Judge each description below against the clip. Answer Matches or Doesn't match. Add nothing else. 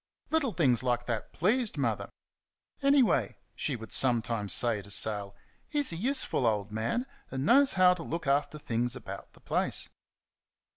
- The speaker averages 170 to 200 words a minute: Doesn't match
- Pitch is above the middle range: Doesn't match